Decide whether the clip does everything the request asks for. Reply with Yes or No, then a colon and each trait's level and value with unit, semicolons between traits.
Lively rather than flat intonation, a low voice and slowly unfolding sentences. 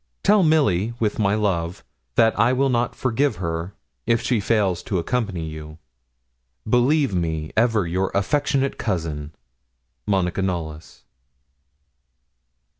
Yes: wide, 6.1 semitones; low, 100 Hz; slow, 115 wpm